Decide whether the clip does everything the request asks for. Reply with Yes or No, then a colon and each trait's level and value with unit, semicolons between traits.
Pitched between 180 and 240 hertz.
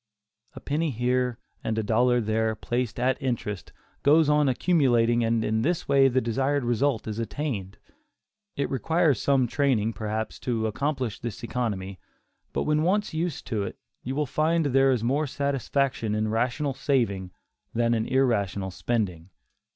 No: low, 125 Hz